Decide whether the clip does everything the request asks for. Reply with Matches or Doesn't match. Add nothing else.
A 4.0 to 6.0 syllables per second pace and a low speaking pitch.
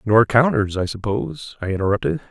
Matches